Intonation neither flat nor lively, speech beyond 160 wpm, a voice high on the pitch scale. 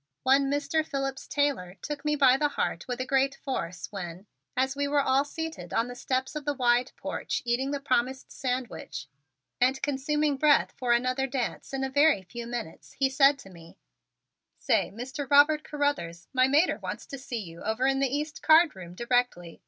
Yes: average, 3.0 semitones; average, 190 wpm; very high, 265 Hz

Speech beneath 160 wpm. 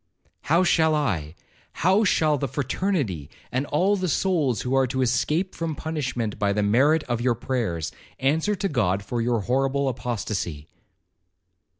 Yes: average, 150 wpm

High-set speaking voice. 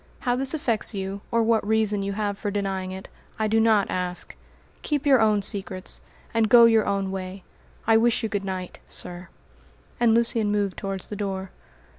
Yes: high, 205 Hz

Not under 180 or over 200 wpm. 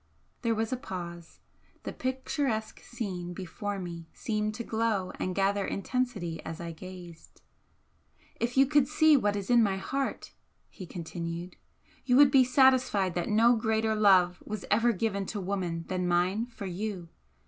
No: average, 160 wpm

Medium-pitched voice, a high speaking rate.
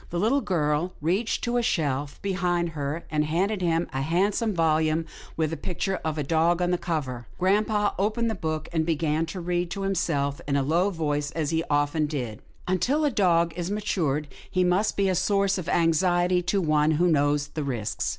Yes: medium, 170 Hz; fast, 210 wpm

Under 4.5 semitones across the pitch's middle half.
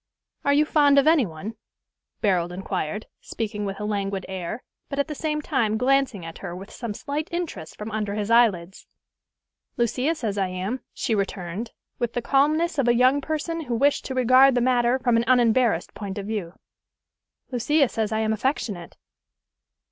No: average, 5.3 semitones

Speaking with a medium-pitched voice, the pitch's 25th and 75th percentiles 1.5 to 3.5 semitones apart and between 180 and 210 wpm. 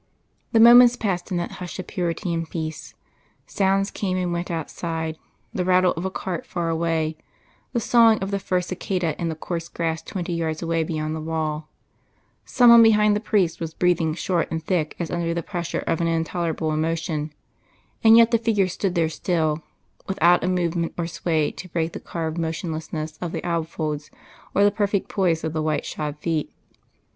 Yes: medium, 170 Hz; narrow, 2.5 semitones; average, 190 wpm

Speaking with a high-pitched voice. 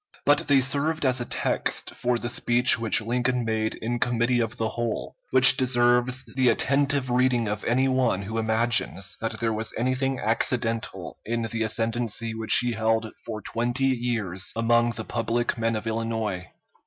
No: low, 120 Hz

